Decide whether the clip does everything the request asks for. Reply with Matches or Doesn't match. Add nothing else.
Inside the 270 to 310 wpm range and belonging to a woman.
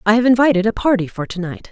Matches